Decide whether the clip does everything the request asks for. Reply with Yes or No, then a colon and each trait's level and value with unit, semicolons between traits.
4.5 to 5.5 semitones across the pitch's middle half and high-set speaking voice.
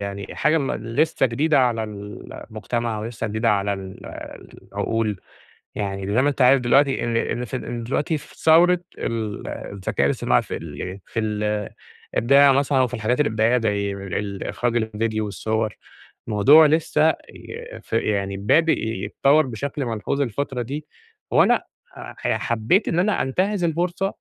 No: average, 5.2 semitones; low, 115 Hz